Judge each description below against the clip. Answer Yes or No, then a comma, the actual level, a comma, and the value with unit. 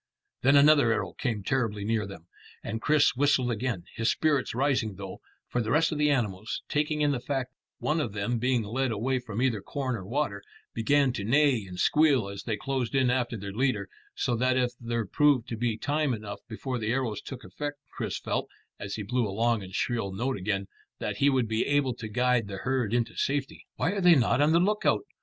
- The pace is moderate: No, fast, 220 wpm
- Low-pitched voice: Yes, low, 125 Hz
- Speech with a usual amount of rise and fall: Yes, average, 4.2 semitones